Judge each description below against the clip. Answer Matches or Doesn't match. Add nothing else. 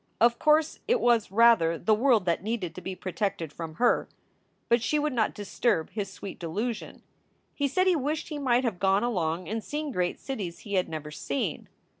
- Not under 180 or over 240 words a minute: Matches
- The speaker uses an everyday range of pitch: Doesn't match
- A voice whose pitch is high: Matches